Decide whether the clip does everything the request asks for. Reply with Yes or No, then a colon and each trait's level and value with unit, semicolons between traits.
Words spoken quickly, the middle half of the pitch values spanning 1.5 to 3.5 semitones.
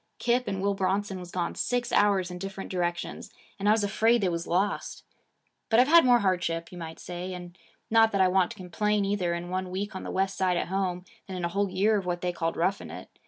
Yes: fast, 245 wpm; narrow, 2.4 semitones